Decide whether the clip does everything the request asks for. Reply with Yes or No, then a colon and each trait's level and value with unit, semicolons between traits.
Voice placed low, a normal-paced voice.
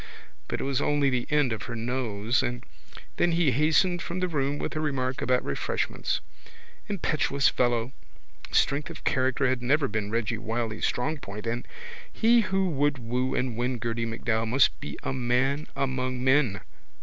Yes: low, 130 Hz; average, 170 wpm